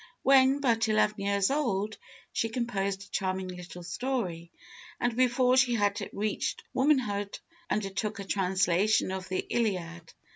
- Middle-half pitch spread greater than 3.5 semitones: Yes, average, 4.2 semitones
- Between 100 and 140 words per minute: Yes, slow, 135 wpm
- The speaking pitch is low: No, high, 205 Hz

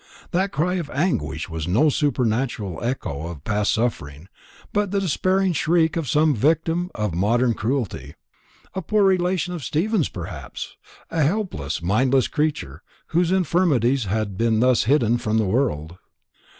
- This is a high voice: No, low, 130 Hz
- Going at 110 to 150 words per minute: Yes, average, 145 wpm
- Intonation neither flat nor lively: No, wide, 8.6 semitones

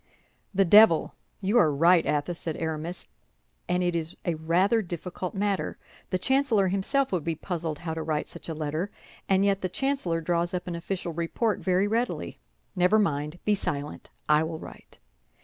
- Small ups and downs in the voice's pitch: No, average, 3.5 semitones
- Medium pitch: Yes, medium, 175 Hz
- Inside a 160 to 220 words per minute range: Yes, average, 175 wpm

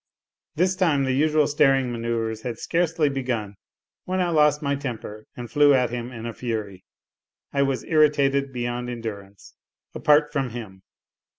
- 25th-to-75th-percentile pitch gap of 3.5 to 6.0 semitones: Yes, average, 4.2 semitones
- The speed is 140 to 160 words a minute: Yes, average, 155 wpm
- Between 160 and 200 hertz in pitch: No, low, 130 Hz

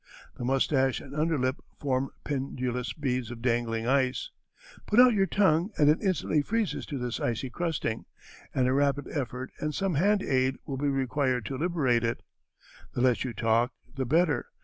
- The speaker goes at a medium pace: Yes, average, 175 wpm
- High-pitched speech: No, low, 135 Hz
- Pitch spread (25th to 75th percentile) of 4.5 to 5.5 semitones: No, average, 3.5 semitones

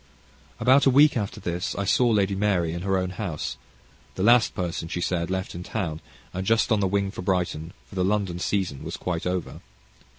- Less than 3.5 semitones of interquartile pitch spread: Yes, average, 2.9 semitones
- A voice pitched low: Yes, very low, 95 Hz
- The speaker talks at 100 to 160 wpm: No, fast, 205 wpm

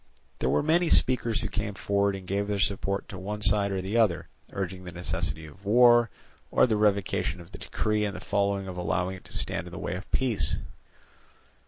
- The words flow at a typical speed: No, fast, 210 wpm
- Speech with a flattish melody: Yes, narrow, 2.3 semitones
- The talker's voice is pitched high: No, low, 100 Hz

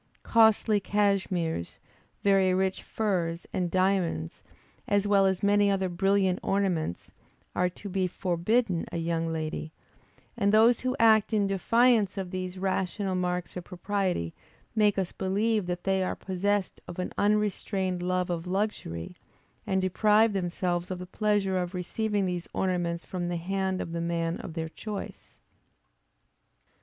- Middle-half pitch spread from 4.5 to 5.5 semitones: No, narrow, 2.4 semitones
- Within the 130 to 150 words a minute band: Yes, average, 145 wpm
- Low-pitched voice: No, high, 190 Hz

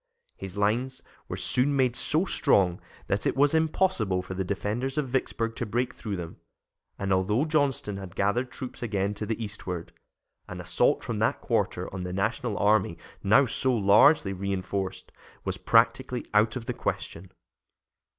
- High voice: No, low, 105 Hz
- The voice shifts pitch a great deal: No, average, 4.8 semitones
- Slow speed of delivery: No, average, 160 wpm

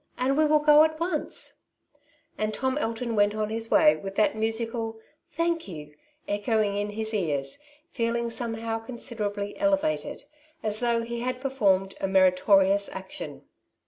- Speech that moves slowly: No, average, 155 wpm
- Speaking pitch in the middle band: No, high, 225 Hz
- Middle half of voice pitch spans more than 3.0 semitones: Yes, average, 4.1 semitones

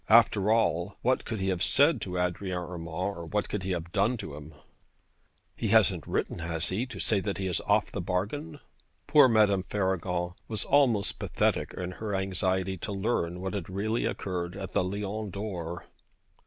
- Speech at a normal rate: Yes, average, 180 wpm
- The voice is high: No, very low, 95 Hz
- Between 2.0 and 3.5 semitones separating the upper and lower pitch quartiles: Yes, average, 3.0 semitones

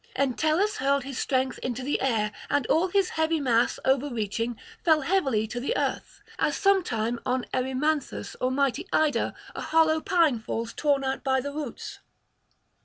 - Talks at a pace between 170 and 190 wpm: No, average, 160 wpm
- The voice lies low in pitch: No, very high, 275 Hz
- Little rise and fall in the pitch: No, average, 4.1 semitones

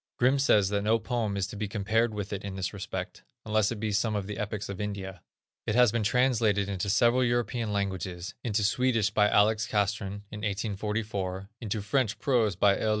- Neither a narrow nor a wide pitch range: No, narrow, 2.2 semitones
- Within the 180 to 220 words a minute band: Yes, average, 200 wpm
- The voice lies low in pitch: Yes, low, 105 Hz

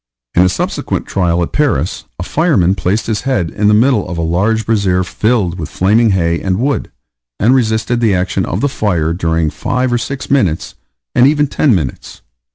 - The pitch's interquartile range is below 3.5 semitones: No, wide, 5.6 semitones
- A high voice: No, low, 100 Hz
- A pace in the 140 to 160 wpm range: No, average, 190 wpm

